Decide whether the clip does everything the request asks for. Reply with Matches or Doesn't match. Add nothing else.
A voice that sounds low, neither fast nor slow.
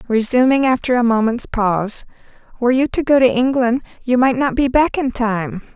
Doesn't match